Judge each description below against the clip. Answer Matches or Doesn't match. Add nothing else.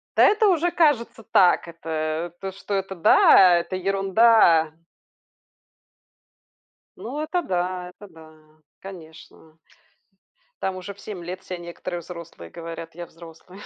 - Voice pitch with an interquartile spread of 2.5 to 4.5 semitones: Matches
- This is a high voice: Doesn't match